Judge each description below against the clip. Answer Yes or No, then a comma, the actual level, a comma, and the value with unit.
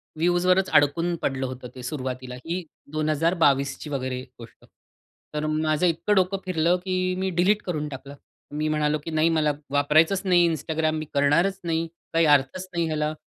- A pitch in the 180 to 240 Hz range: No, medium, 155 Hz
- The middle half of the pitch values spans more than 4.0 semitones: No, average, 3.5 semitones